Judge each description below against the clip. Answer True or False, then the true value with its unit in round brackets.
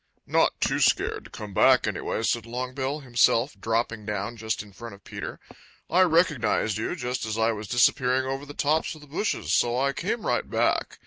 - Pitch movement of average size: True (4.3 semitones)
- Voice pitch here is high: False (120 Hz)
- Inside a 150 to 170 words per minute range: False (195 wpm)